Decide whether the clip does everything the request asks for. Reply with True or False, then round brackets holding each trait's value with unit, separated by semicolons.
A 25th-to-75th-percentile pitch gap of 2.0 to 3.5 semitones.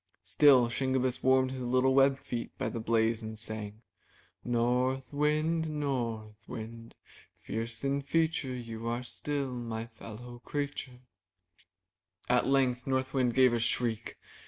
True (2.6 semitones)